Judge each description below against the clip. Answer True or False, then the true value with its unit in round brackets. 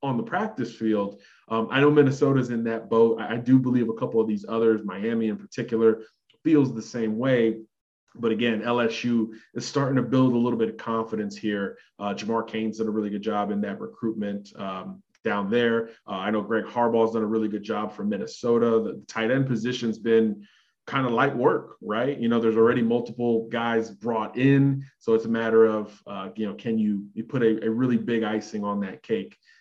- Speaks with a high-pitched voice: False (115 Hz)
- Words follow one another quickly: True (210 wpm)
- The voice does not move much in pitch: True (1.7 semitones)